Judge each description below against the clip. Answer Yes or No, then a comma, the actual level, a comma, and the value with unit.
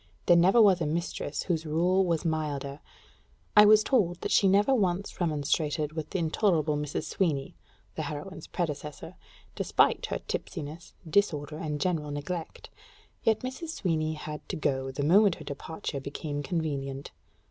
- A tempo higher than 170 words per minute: No, average, 150 wpm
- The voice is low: No, medium, 160 Hz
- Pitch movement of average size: Yes, average, 3.9 semitones